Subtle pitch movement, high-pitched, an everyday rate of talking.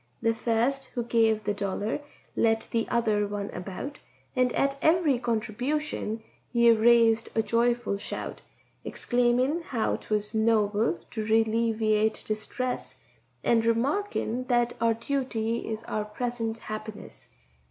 No: narrow, 2.0 semitones; high, 230 Hz; slow, 125 wpm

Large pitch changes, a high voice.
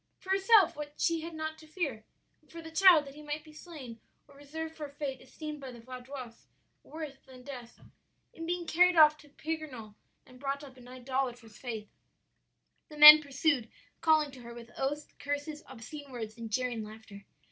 No: average, 3.9 semitones; very high, 285 Hz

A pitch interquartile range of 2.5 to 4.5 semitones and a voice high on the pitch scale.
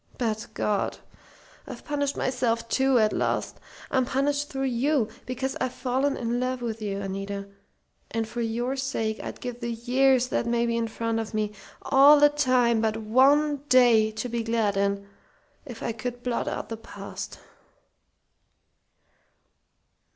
Yes: average, 2.8 semitones; high, 240 Hz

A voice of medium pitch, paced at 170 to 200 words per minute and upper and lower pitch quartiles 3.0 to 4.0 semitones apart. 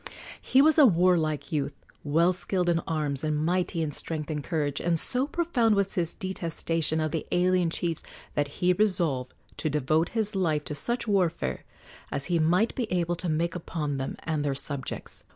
Yes: medium, 165 Hz; average, 185 wpm; average, 3.4 semitones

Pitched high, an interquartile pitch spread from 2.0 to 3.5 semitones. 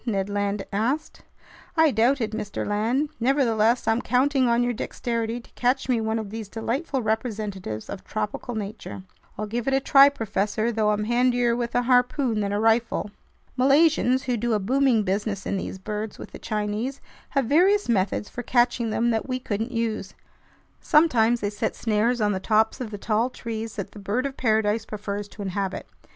Yes: high, 225 Hz; average, 3.1 semitones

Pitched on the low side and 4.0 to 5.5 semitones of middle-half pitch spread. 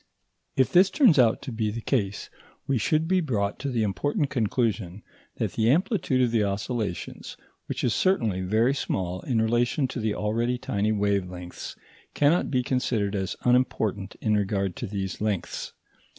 Yes: low, 110 Hz; average, 4.4 semitones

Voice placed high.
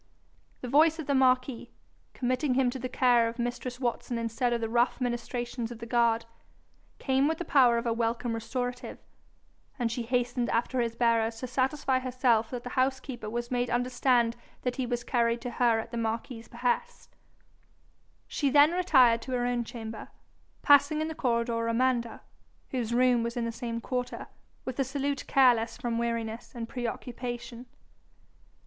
Yes: high, 245 Hz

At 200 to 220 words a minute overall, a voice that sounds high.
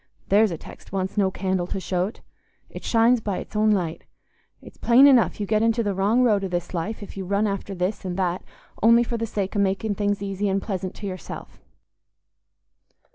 Yes: fast, 205 wpm; high, 200 Hz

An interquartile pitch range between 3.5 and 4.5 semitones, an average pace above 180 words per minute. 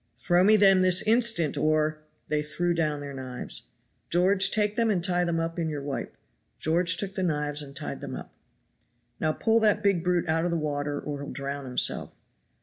Yes: average, 4.0 semitones; fast, 205 wpm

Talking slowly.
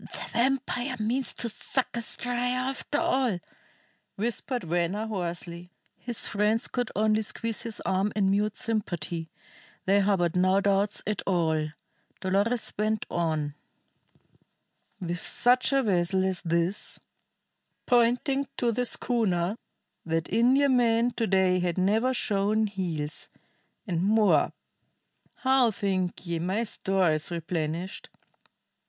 Yes: slow, 120 wpm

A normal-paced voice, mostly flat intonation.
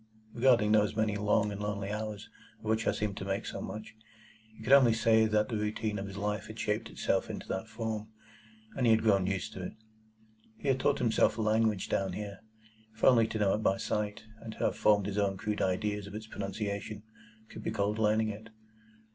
No: fast, 215 wpm; narrow, 1.4 semitones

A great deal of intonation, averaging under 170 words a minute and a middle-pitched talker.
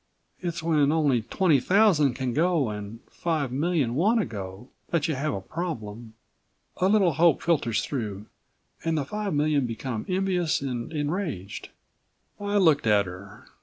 Yes: wide, 6.8 semitones; average, 155 wpm; medium, 145 Hz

